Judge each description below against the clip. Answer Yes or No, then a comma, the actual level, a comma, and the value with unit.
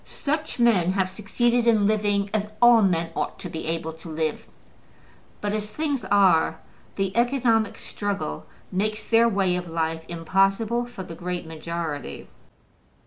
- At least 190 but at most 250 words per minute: No, average, 145 wpm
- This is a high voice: Yes, high, 195 Hz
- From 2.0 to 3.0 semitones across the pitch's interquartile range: No, average, 5.0 semitones